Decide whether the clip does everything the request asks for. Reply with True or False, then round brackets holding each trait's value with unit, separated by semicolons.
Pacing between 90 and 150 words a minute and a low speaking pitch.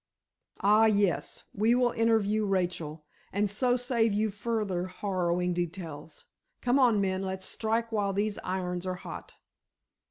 False (135 wpm; 200 Hz)